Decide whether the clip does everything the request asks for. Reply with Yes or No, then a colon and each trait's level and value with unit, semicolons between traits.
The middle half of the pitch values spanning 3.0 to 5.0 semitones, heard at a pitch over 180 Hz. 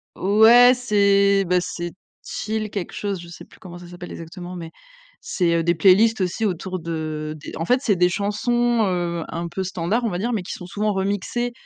Yes: average, 3.6 semitones; high, 190 Hz